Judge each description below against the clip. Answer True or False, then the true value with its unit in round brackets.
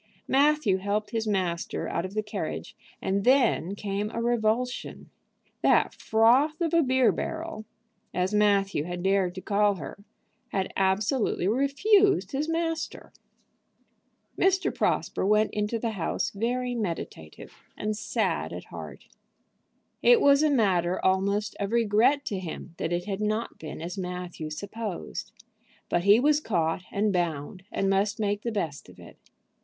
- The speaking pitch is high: True (210 Hz)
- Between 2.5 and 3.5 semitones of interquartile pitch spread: False (4.6 semitones)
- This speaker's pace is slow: False (150 wpm)